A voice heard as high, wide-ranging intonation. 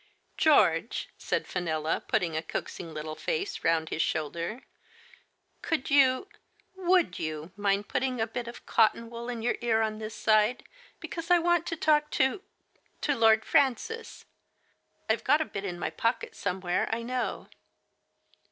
Yes: high, 230 Hz; wide, 7.8 semitones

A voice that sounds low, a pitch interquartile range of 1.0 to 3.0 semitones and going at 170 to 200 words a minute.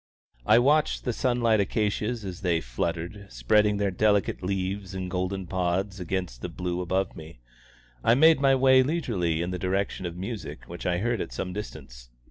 No: very low, 95 Hz; average, 3.6 semitones; average, 175 wpm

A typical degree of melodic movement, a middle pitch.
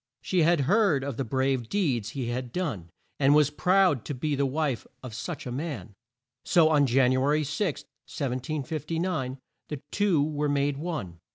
Yes: average, 3.6 semitones; medium, 145 Hz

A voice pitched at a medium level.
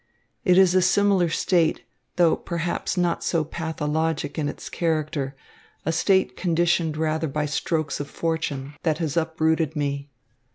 Yes: medium, 160 Hz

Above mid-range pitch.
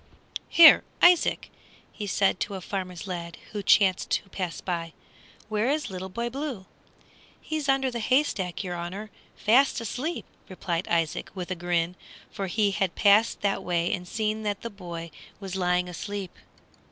Yes: high, 195 Hz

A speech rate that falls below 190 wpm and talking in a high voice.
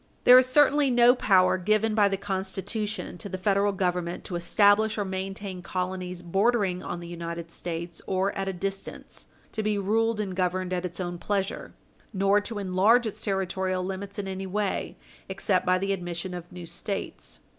Yes: average, 175 wpm; high, 195 Hz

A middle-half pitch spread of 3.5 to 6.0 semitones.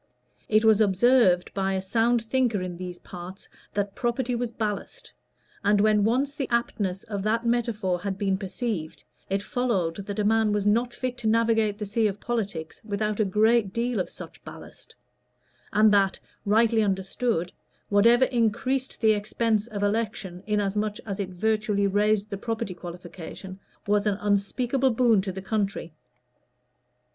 No: average, 2.8 semitones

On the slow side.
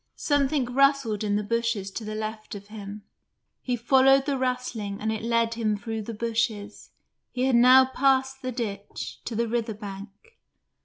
No: average, 170 wpm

